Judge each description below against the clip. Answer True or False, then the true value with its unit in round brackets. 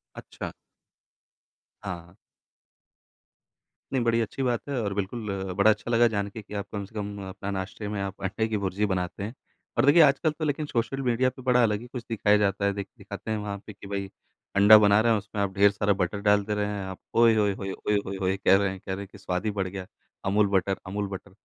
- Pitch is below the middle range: True (100 Hz)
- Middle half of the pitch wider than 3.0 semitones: False (2.4 semitones)